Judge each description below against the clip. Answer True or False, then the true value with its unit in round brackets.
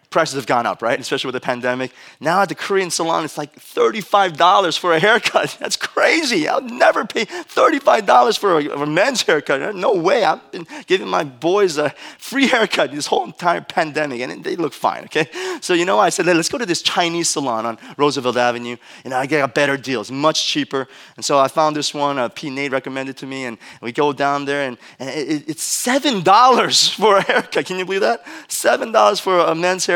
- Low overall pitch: False (155 Hz)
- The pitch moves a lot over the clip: True (6.4 semitones)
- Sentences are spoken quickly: True (220 wpm)